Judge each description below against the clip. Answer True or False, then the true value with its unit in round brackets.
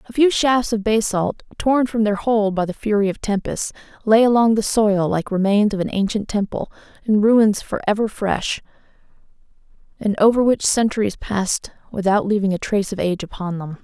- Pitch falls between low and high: False (210 Hz)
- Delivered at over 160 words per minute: True (180 wpm)